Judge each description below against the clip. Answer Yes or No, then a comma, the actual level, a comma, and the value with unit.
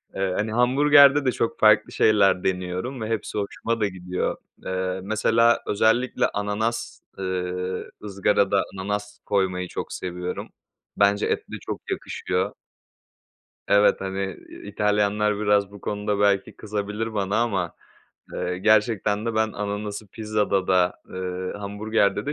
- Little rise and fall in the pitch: Yes, narrow, 2.3 semitones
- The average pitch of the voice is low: Yes, low, 105 Hz